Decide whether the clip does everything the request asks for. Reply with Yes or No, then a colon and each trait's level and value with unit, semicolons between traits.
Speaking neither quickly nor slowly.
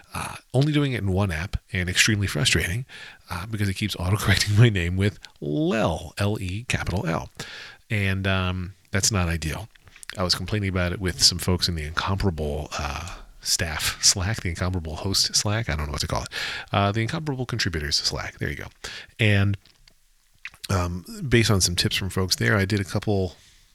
Yes: average, 185 wpm